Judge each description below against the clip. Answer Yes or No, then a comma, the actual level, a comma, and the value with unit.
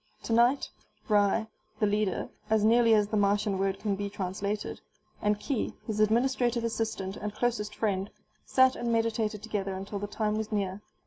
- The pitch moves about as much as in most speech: No, narrow, 2.0 semitones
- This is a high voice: Yes, high, 210 Hz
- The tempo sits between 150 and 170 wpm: Yes, average, 165 wpm